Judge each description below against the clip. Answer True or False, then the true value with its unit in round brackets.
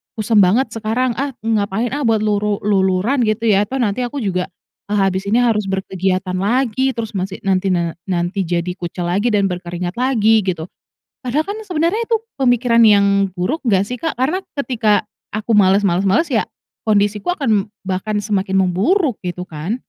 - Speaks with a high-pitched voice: True (210 Hz)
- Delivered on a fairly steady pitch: False (4.2 semitones)